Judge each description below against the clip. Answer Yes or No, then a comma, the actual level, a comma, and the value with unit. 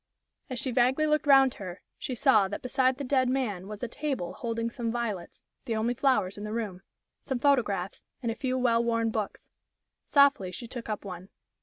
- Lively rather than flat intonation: No, average, 3.7 semitones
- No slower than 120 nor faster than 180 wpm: No, average, 195 wpm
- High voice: Yes, high, 235 Hz